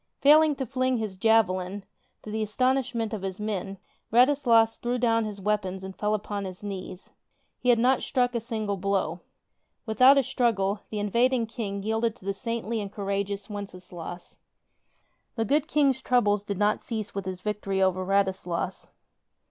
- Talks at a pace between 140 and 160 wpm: No, average, 175 wpm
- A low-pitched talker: No, high, 210 Hz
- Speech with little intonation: No, average, 3.4 semitones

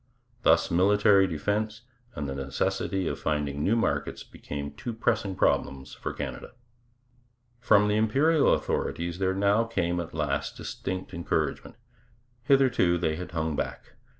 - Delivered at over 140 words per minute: No, slow, 135 wpm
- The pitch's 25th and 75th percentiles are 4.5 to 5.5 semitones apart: Yes, average, 5.1 semitones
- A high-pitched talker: No, very low, 95 Hz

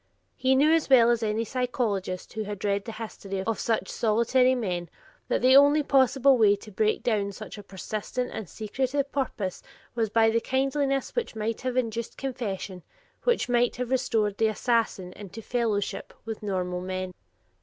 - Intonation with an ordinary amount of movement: Yes, average, 3.9 semitones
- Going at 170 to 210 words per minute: Yes, average, 175 wpm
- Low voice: No, high, 225 Hz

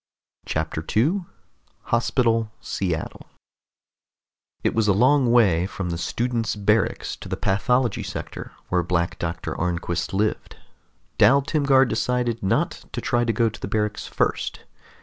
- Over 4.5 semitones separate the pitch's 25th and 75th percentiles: Yes, average, 5.1 semitones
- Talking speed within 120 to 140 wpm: Yes, slow, 135 wpm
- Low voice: Yes, low, 110 Hz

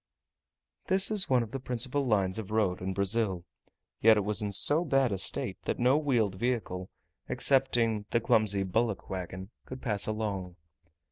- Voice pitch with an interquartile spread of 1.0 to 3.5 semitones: No, average, 4.5 semitones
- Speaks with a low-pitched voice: Yes, low, 110 Hz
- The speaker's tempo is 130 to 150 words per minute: No, average, 165 wpm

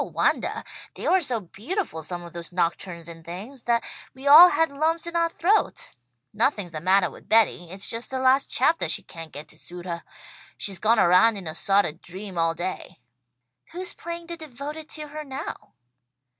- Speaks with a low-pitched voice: No, high, 215 Hz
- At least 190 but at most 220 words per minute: Yes, average, 195 wpm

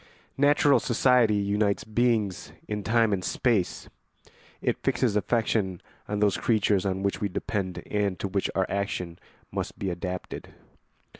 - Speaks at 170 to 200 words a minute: No, average, 145 wpm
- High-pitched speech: No, low, 100 Hz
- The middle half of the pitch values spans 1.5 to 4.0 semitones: Yes, average, 2.9 semitones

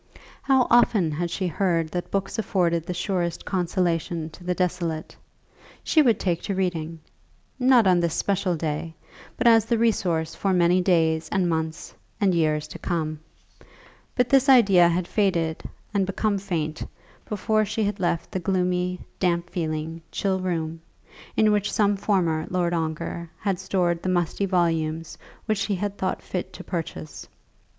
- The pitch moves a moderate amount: Yes, average, 3.1 semitones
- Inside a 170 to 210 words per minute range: No, average, 160 wpm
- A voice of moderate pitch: Yes, medium, 180 Hz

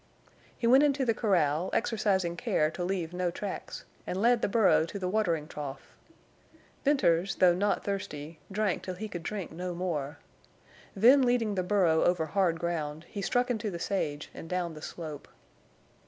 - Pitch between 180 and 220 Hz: Yes, medium, 185 Hz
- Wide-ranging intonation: No, average, 4.2 semitones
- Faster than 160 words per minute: Yes, average, 170 wpm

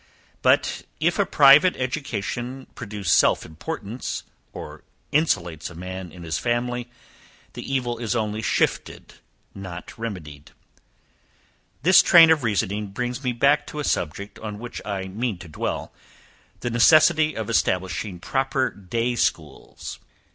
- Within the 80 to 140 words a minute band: Yes, slow, 135 wpm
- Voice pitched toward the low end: Yes, low, 115 Hz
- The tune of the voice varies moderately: No, wide, 5.8 semitones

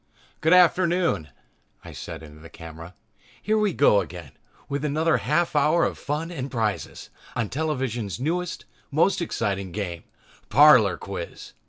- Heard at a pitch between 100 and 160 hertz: Yes, medium, 140 Hz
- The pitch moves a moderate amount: No, wide, 9.0 semitones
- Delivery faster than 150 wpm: No, average, 140 wpm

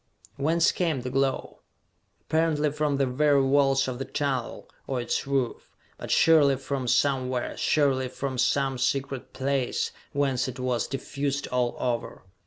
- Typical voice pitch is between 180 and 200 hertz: No, low, 135 Hz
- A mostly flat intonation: Yes, narrow, 1.8 semitones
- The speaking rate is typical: Yes, average, 145 wpm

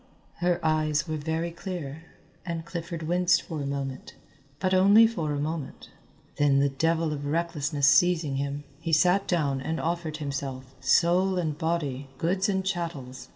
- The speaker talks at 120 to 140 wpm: No, average, 155 wpm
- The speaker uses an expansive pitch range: No, average, 3.4 semitones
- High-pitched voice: No, medium, 160 Hz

